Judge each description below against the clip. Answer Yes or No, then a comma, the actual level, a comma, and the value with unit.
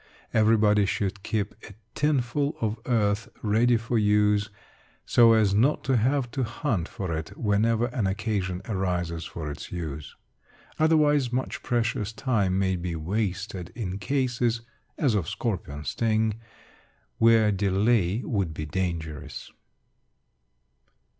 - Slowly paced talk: Yes, slow, 125 wpm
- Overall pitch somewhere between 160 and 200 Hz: No, low, 105 Hz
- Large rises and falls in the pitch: No, average, 3.8 semitones